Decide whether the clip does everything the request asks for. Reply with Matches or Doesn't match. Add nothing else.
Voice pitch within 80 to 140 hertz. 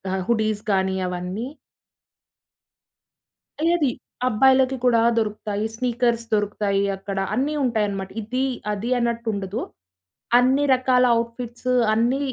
Doesn't match